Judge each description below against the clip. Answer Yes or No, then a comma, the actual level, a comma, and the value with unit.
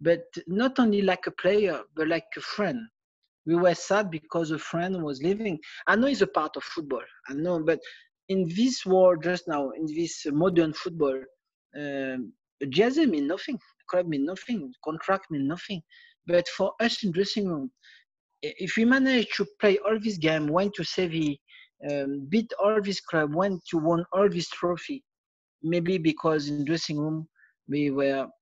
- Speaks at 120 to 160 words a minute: No, average, 175 wpm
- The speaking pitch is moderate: Yes, medium, 180 Hz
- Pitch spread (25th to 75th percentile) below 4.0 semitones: No, average, 4.7 semitones